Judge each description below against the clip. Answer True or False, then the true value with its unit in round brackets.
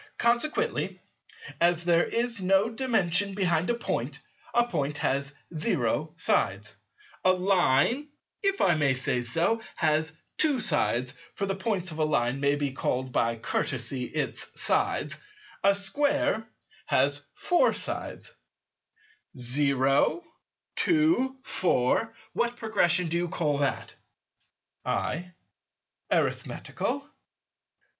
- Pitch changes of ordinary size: False (8.2 semitones)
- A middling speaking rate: False (115 wpm)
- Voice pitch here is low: False (175 Hz)